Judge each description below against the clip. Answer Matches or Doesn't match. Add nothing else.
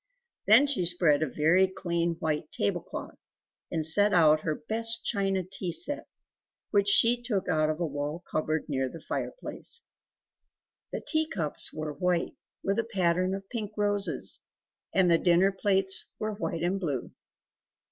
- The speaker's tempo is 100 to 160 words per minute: Matches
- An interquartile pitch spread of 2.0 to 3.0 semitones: Doesn't match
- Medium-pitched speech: Matches